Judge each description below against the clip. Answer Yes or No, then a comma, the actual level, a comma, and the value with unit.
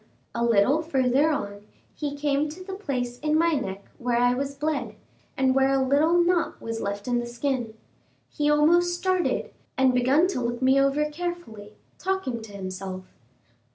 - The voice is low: No, very high, 270 Hz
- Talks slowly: No, average, 170 wpm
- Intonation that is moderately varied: Yes, average, 4.4 semitones